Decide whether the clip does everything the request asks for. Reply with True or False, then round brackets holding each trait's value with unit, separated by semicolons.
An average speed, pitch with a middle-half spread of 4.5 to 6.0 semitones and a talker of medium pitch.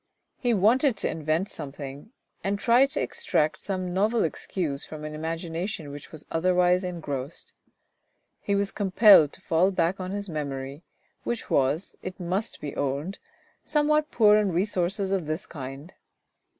True (150 wpm; 4.8 semitones; 180 Hz)